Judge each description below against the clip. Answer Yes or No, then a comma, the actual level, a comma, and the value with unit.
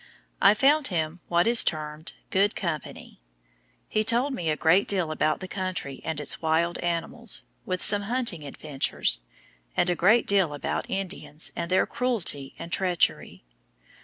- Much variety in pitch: No, average, 4.5 semitones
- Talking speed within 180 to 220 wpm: No, average, 155 wpm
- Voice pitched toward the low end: No, medium, 175 Hz